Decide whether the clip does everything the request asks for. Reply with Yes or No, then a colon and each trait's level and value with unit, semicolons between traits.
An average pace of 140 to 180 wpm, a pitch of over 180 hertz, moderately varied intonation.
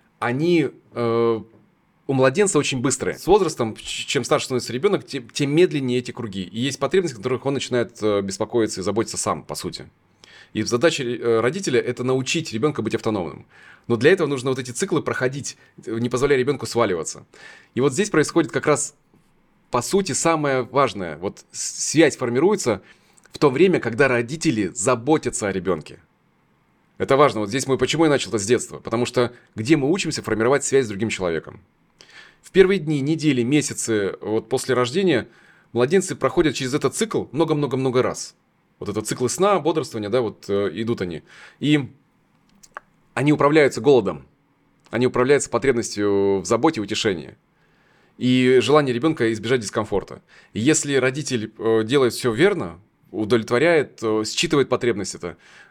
No: average, 155 wpm; low, 130 Hz; average, 4.7 semitones